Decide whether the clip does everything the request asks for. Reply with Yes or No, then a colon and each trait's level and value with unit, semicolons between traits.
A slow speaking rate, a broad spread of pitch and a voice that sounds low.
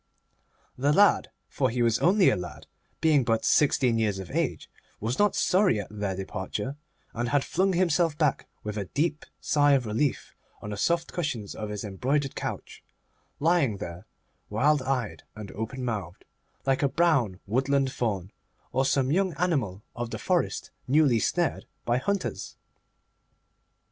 No: average, 155 wpm; wide, 6.1 semitones; low, 130 Hz